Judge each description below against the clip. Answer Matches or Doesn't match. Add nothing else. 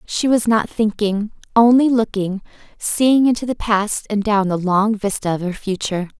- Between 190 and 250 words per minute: Doesn't match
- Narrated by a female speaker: Matches